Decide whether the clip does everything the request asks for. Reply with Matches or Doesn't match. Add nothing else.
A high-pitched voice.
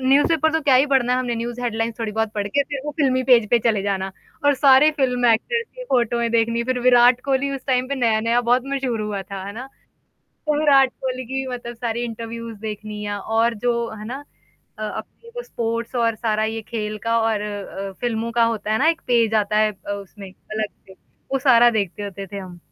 Matches